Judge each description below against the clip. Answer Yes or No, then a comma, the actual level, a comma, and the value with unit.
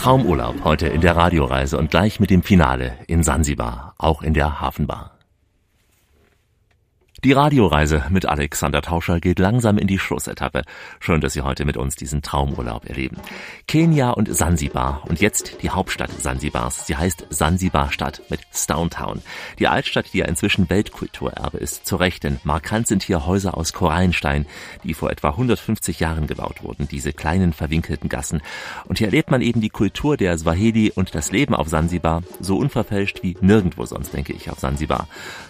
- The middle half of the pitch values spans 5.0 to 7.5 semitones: Yes, average, 5.3 semitones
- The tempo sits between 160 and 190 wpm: Yes, average, 165 wpm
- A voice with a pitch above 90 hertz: No, very low, 85 Hz